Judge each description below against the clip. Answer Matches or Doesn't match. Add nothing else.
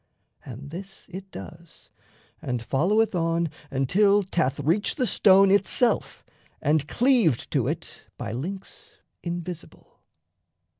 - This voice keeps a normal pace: Doesn't match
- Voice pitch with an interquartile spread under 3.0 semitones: Doesn't match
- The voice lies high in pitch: Doesn't match